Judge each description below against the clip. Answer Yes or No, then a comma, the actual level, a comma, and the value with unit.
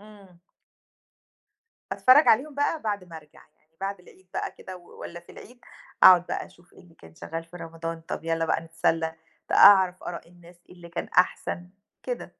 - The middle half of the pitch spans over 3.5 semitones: No, average, 2.9 semitones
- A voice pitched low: No, medium, 175 Hz